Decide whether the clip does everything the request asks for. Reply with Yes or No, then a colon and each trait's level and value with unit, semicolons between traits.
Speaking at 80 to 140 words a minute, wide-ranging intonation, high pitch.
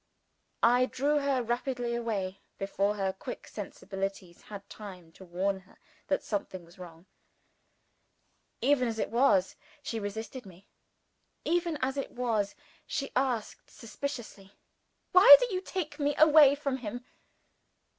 Yes: slow, 135 wpm; wide, 5.9 semitones; high, 230 Hz